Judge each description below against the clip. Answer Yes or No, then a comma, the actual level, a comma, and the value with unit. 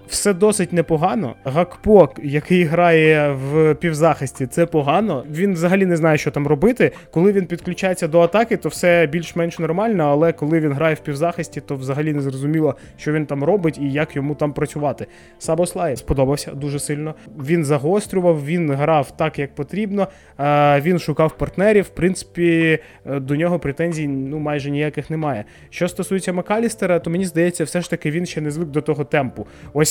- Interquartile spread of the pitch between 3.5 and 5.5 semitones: No, average, 3.0 semitones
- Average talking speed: No, fast, 175 wpm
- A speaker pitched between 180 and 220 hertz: No, medium, 160 Hz